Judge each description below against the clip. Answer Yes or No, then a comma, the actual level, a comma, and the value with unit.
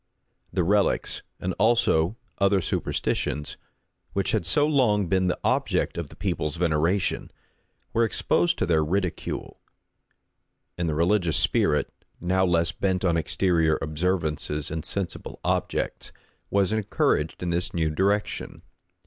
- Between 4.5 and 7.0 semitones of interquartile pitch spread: No, average, 3.6 semitones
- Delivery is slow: Yes, slow, 130 wpm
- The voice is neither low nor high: No, very low, 90 Hz